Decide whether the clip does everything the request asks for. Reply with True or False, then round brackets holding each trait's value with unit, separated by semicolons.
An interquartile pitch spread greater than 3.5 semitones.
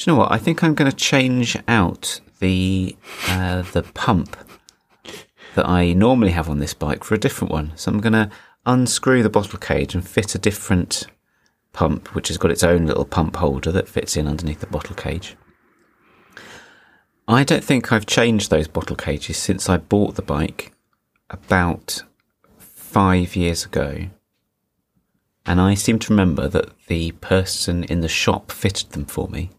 True (4.7 semitones)